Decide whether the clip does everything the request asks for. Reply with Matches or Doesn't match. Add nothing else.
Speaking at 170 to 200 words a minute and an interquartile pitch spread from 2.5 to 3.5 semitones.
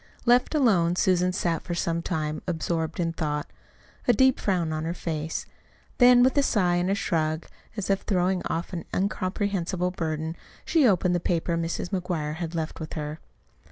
Matches